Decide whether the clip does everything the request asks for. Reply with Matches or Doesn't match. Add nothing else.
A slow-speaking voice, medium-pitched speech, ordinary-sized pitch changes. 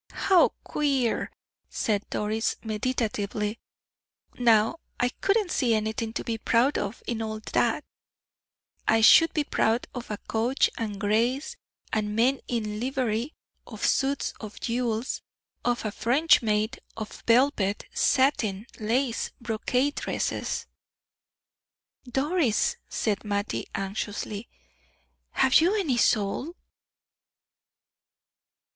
Doesn't match